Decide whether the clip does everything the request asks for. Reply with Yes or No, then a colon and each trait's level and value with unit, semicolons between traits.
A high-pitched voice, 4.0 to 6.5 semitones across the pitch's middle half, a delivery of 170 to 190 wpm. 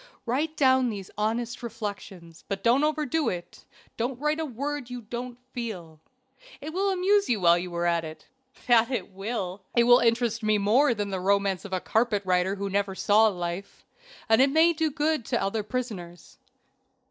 Yes: high, 225 Hz; average, 5.0 semitones; average, 180 wpm